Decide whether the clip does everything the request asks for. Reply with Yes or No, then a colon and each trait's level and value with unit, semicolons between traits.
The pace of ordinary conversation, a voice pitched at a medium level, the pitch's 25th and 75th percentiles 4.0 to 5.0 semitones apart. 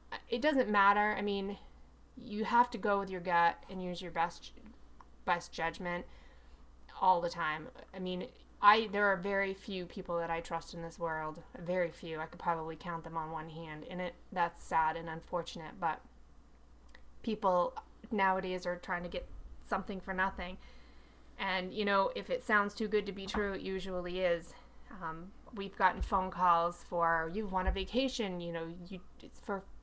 No: average, 180 wpm; medium, 180 Hz; average, 3.1 semitones